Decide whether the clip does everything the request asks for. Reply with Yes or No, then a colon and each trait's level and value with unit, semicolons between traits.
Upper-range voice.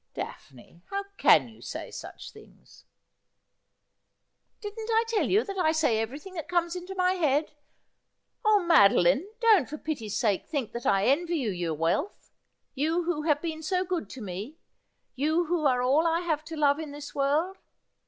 Yes: very high, 310 Hz